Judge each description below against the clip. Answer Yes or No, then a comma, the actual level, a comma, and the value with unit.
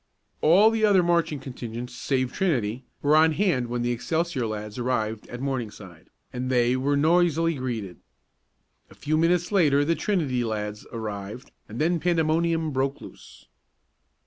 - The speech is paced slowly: No, average, 145 wpm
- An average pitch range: No, wide, 5.7 semitones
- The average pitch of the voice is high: No, low, 135 Hz